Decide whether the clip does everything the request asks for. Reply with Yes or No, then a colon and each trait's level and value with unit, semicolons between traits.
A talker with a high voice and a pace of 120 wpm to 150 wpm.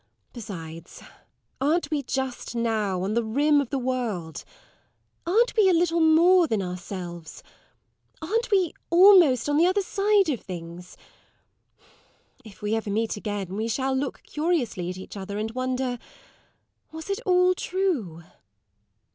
Yes: very high, 255 Hz; average, 140 wpm